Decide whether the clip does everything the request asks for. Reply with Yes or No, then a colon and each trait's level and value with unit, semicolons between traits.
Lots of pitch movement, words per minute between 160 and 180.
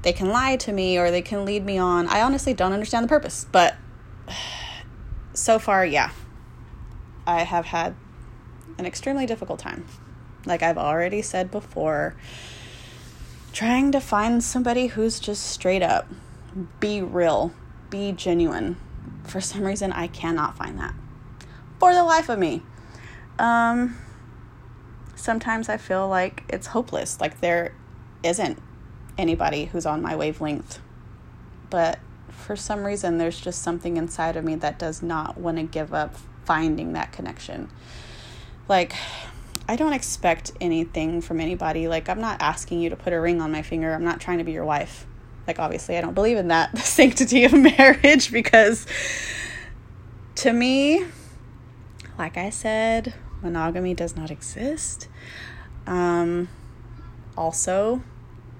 No: wide, 5.7 semitones; average, 145 wpm